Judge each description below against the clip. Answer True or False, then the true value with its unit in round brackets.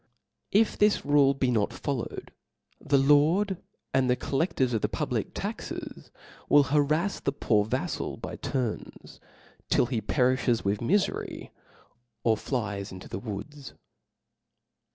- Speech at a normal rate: False (130 wpm)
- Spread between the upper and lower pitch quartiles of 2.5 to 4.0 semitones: False (4.4 semitones)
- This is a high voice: False (135 Hz)